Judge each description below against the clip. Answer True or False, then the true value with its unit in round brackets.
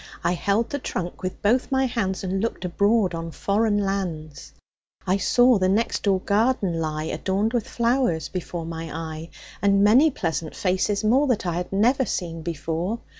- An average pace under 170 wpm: False (175 wpm)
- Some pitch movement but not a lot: True (5.0 semitones)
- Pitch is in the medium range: False (195 Hz)